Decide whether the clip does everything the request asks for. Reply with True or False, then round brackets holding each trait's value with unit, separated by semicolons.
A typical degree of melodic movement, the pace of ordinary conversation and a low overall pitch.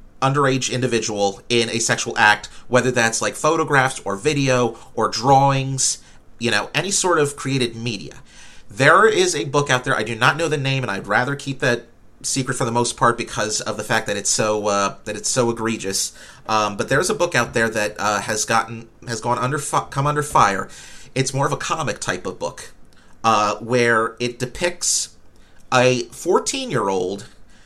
True (3.9 semitones; 195 wpm; 120 Hz)